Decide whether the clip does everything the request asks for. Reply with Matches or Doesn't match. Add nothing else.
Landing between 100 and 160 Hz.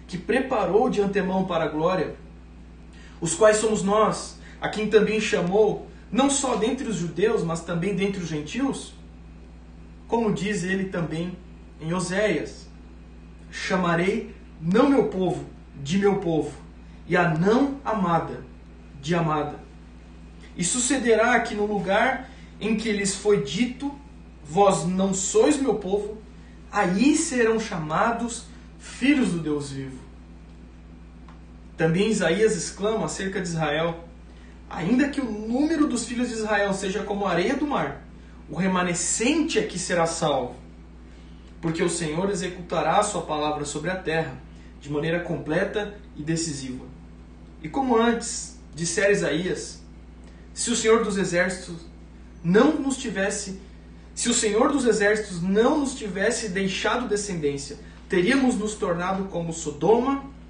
Doesn't match